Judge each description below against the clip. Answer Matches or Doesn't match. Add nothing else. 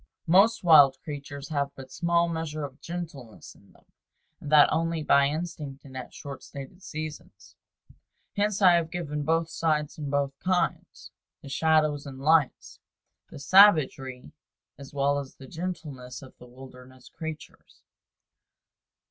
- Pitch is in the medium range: Matches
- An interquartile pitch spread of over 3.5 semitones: Doesn't match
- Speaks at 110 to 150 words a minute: Matches